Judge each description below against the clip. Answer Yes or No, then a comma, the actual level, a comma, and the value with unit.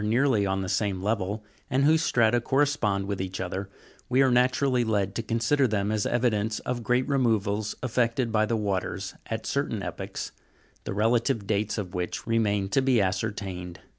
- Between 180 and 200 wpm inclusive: No, average, 170 wpm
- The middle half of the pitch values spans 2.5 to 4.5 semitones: Yes, average, 3.6 semitones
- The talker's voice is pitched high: No, low, 110 Hz